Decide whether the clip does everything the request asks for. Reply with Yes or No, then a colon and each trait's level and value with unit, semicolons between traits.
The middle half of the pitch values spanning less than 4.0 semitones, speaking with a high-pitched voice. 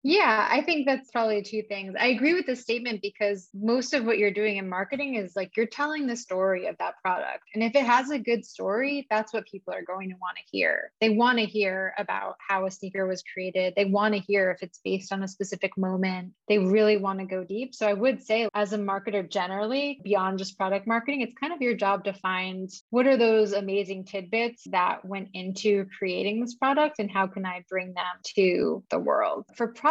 Yes: average, 3.5 semitones; high, 205 Hz